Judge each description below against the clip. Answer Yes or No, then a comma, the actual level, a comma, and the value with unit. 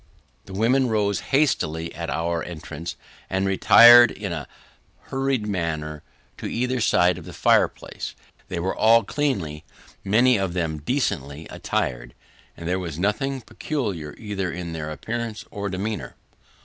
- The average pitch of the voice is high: No, very low, 95 Hz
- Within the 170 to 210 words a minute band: No, average, 140 wpm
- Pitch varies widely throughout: Yes, wide, 5.9 semitones